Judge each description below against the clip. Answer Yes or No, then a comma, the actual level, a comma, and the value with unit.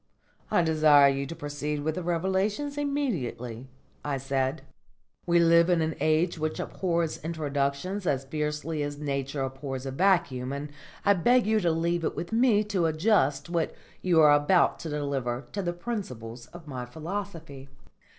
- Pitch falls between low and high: Yes, medium, 155 Hz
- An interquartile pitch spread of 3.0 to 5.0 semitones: Yes, average, 4.3 semitones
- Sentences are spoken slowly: No, average, 160 wpm